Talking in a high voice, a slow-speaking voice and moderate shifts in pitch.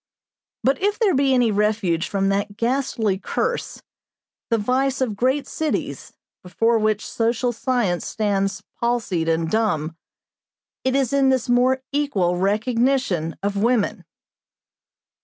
Yes: high, 230 Hz; slow, 125 wpm; average, 4.6 semitones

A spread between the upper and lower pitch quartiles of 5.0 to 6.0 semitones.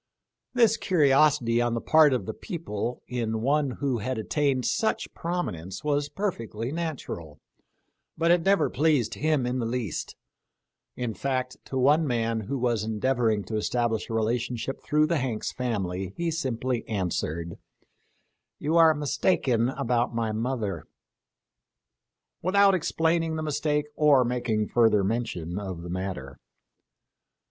Yes: average, 5.3 semitones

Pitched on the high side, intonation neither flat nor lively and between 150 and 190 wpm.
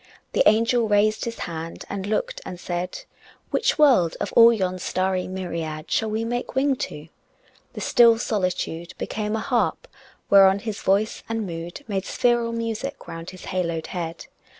Yes: high, 205 Hz; average, 4.5 semitones; average, 160 wpm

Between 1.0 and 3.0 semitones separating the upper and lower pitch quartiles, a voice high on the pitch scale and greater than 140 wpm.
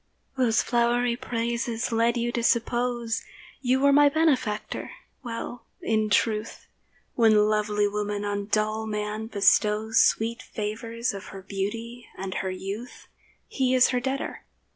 No: narrow, 2.4 semitones; high, 225 Hz; slow, 135 wpm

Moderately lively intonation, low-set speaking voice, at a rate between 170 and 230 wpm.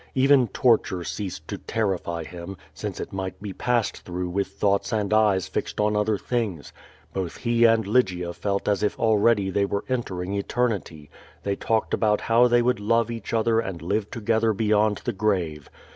Yes: average, 3.1 semitones; low, 105 Hz; average, 175 wpm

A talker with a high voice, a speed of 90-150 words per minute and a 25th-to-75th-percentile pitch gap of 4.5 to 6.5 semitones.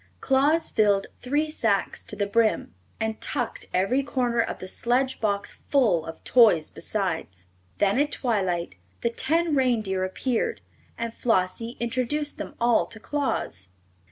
Yes: high, 230 Hz; average, 140 wpm; average, 5.1 semitones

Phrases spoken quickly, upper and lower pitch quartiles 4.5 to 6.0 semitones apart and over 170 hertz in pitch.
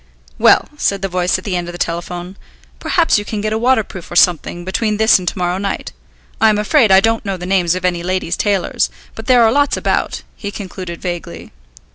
No: fast, 220 wpm; average, 3.3 semitones; high, 190 Hz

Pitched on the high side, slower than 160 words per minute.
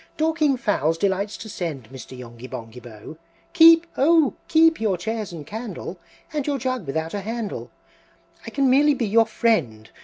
No: high, 215 Hz; average, 165 wpm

